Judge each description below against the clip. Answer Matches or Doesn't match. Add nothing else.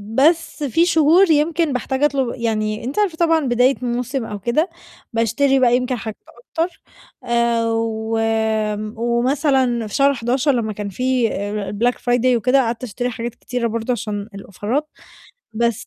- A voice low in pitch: Doesn't match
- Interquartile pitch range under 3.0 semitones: Doesn't match